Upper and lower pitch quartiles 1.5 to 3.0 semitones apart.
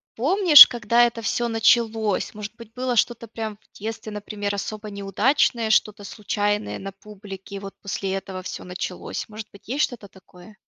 Yes: narrow, 2.5 semitones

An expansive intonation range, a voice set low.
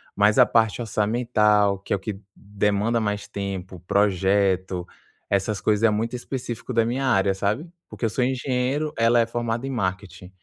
No: average, 3.2 semitones; low, 105 Hz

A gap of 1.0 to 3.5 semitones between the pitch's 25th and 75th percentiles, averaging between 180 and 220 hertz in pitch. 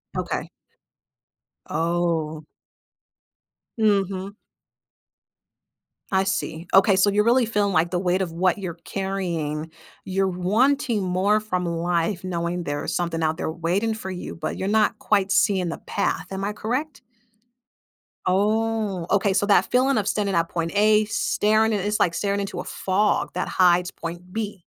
Yes: average, 3.2 semitones; high, 190 Hz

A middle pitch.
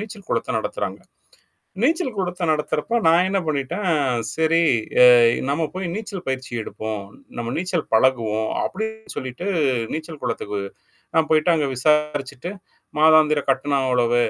Yes: medium, 155 Hz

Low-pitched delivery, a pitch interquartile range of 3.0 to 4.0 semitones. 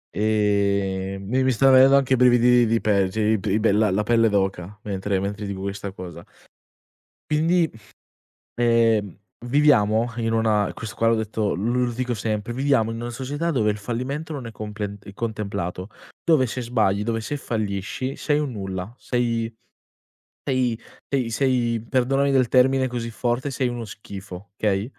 Yes: low, 115 Hz; average, 3.6 semitones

